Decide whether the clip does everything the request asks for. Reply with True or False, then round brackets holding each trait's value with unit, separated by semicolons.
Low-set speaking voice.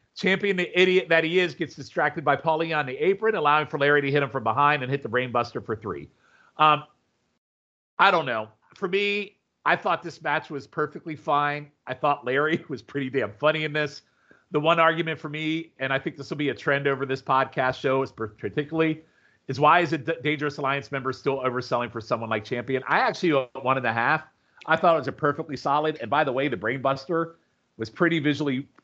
False (145 Hz)